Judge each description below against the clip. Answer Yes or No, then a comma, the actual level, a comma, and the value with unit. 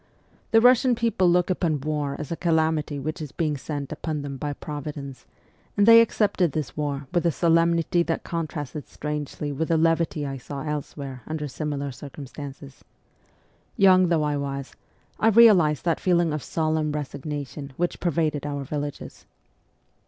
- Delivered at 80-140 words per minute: No, average, 160 wpm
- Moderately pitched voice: Yes, medium, 150 Hz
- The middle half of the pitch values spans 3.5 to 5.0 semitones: No, average, 2.9 semitones